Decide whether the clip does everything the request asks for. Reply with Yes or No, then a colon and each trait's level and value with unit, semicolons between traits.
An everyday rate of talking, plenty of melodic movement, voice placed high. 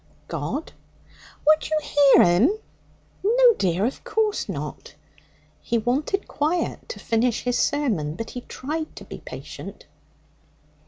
No: slow, 125 wpm; wide, 6.0 semitones; very high, 285 Hz